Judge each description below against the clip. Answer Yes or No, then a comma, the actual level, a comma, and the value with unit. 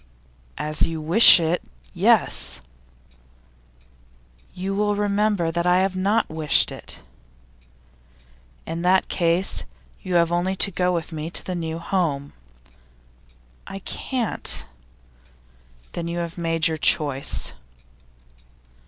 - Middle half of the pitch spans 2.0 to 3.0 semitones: Yes, average, 2.7 semitones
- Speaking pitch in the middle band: Yes, medium, 175 Hz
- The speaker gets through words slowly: Yes, slow, 115 wpm